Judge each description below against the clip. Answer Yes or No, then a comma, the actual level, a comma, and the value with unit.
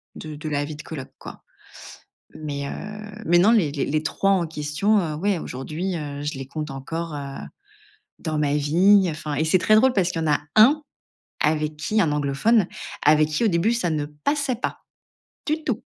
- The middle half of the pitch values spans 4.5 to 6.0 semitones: Yes, average, 5.0 semitones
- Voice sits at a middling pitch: Yes, medium, 155 Hz